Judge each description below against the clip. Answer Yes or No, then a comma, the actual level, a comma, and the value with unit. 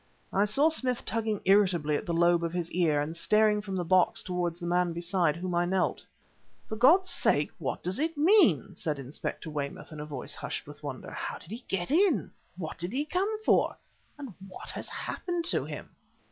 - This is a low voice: No, medium, 185 Hz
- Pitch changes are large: Yes, wide, 6.9 semitones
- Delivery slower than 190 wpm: No, average, 200 wpm